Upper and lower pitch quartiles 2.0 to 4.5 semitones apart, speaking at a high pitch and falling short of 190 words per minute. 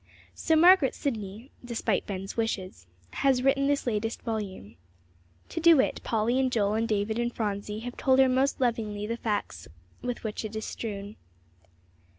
Yes: average, 3.8 semitones; high, 225 Hz; average, 165 wpm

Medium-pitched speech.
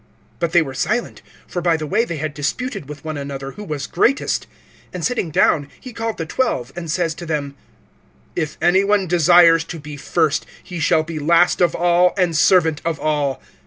Yes: medium, 165 Hz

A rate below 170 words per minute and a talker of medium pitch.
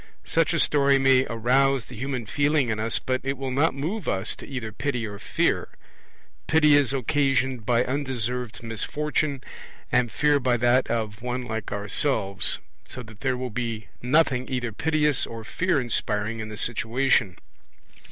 No: average, 160 wpm; low, 125 Hz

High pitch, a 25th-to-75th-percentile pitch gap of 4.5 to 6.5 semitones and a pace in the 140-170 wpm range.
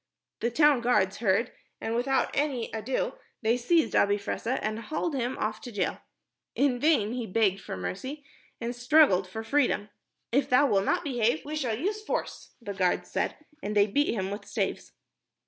No: high, 235 Hz; average, 5.1 semitones; average, 180 wpm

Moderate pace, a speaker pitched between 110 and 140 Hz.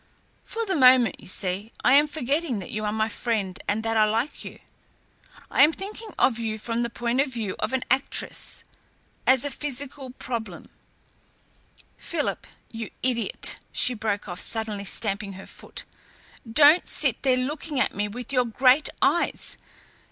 No: average, 165 wpm; high, 240 Hz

